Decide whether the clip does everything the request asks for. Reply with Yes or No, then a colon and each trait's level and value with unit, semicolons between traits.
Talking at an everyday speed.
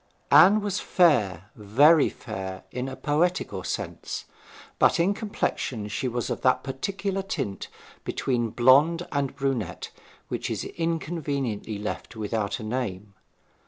No: slow, 125 wpm